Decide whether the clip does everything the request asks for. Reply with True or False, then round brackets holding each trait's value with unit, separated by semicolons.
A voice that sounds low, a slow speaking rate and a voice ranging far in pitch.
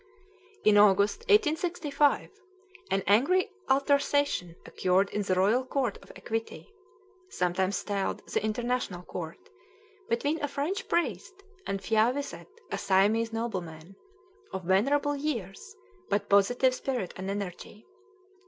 False (225 Hz; 115 wpm; 6.6 semitones)